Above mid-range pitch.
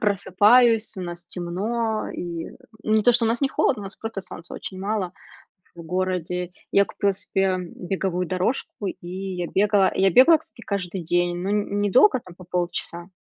Yes: high, 195 Hz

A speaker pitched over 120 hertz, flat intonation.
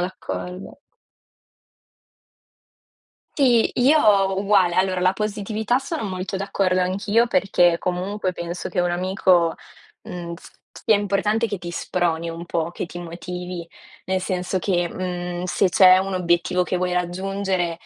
Yes: medium, 185 Hz; narrow, 2.0 semitones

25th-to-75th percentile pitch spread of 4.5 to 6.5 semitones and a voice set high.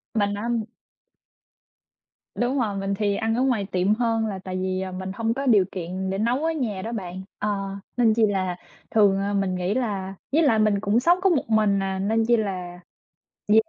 No: average, 3.2 semitones; high, 205 Hz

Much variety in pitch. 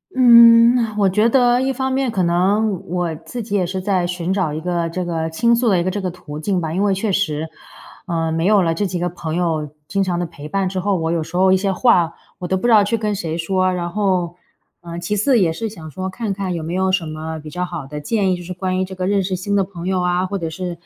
No: average, 3.0 semitones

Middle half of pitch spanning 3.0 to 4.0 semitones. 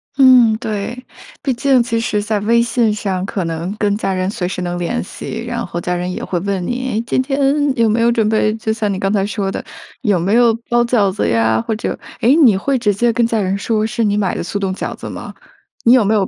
Yes: average, 3.5 semitones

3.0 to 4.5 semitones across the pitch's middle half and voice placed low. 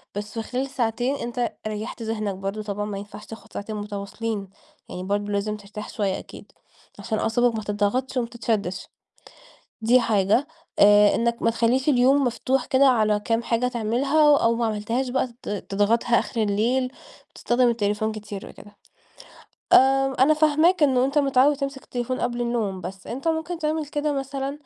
No: average, 4.2 semitones; high, 235 Hz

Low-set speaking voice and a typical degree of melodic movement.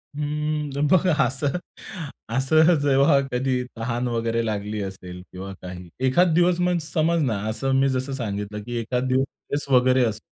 Yes: low, 130 Hz; average, 4.7 semitones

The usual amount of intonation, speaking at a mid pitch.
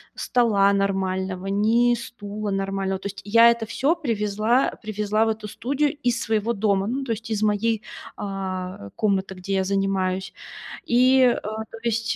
No: average, 3.0 semitones; high, 210 Hz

